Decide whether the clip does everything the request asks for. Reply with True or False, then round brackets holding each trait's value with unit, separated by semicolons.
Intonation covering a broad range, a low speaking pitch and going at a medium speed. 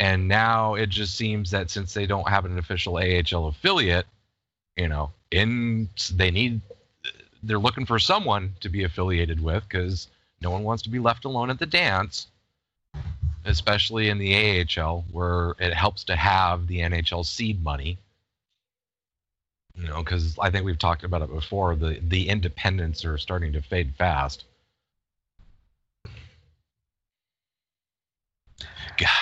False (3.4 semitones; 90 Hz; 145 wpm)